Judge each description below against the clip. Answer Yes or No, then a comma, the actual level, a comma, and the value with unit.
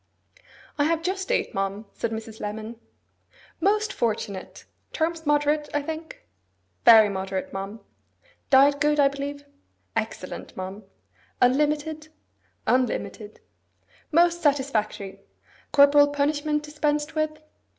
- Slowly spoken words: Yes, slow, 105 wpm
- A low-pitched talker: No, very high, 285 Hz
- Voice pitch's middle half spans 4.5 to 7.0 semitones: Yes, wide, 5.6 semitones